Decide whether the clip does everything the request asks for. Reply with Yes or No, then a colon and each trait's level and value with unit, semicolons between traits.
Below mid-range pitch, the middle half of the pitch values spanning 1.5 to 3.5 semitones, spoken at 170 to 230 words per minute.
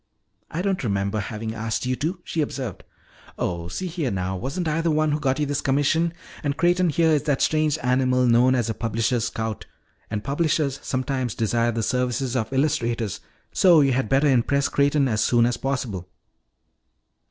No: low, 130 Hz; average, 4.4 semitones; average, 180 wpm